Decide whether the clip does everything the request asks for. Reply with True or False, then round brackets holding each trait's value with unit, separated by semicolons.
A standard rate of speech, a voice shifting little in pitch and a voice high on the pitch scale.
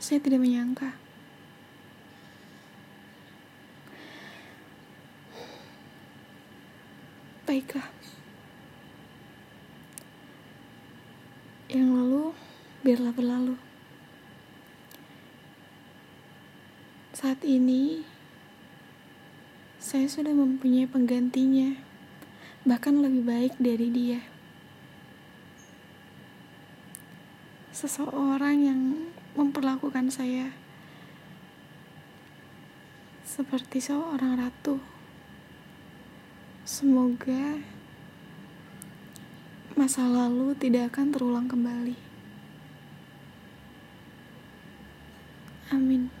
False (45 wpm; 1.9 semitones; 260 Hz)